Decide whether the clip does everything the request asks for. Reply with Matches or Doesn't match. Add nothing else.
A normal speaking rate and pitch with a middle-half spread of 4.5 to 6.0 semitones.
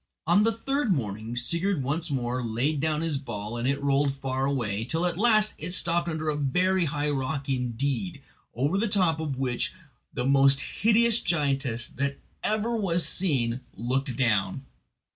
Matches